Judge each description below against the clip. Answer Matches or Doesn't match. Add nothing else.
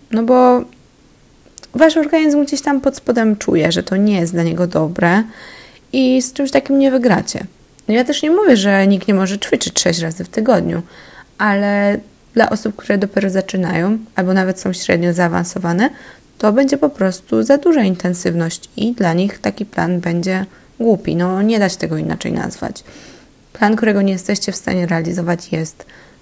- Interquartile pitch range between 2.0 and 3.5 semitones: Doesn't match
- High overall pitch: Matches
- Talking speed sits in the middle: Doesn't match